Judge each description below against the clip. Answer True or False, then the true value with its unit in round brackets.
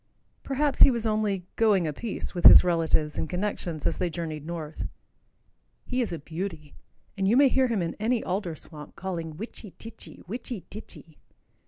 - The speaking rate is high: False (175 wpm)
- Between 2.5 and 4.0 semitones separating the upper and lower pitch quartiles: False (5.4 semitones)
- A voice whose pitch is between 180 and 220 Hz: True (185 Hz)